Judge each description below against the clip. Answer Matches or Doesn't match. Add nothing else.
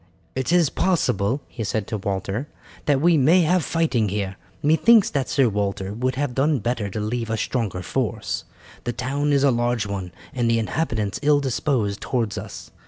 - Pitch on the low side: Matches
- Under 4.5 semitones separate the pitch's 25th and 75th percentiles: Doesn't match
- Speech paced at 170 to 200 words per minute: Matches